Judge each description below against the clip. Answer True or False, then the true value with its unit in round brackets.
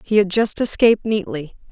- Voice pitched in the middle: False (200 Hz)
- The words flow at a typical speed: True (175 wpm)